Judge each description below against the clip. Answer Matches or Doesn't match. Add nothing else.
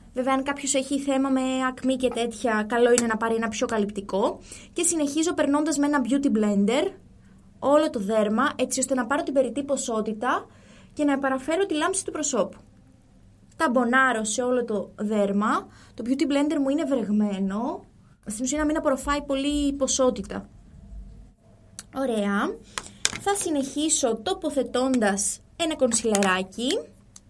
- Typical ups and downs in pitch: Matches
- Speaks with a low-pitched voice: Doesn't match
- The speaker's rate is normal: Matches